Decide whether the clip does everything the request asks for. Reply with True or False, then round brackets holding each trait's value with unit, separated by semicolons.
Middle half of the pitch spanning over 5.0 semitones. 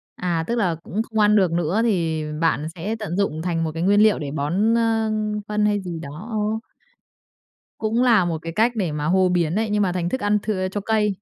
False (4.4 semitones)